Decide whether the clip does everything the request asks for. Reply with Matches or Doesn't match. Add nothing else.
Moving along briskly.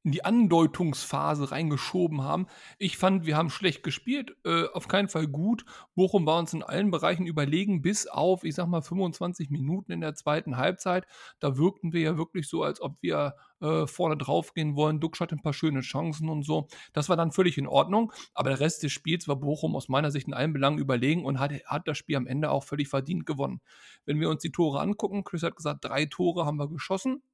Matches